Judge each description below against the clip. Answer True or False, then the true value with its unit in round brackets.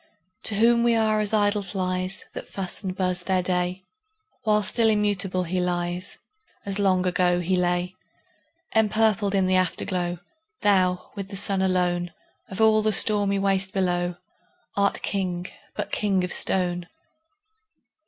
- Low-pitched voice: False (190 Hz)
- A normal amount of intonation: False (2.2 semitones)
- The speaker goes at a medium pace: True (145 wpm)